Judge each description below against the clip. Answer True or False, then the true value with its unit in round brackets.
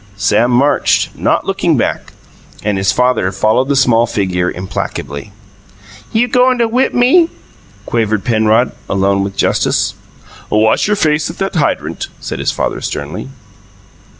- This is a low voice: True (115 Hz)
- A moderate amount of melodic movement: False (8.1 semitones)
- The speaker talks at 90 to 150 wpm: True (140 wpm)